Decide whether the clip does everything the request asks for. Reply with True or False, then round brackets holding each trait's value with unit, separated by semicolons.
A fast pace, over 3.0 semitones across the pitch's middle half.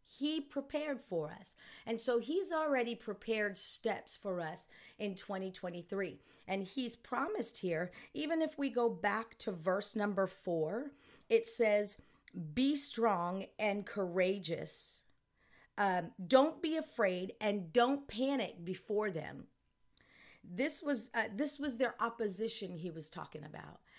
False (135 wpm; 5.6 semitones)